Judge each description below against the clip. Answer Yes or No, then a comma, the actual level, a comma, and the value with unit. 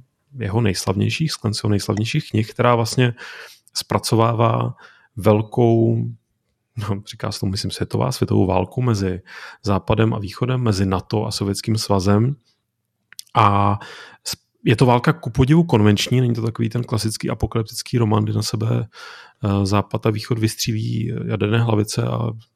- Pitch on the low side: Yes, low, 110 Hz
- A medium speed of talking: Yes, average, 135 wpm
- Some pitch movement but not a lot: No, narrow, 2.3 semitones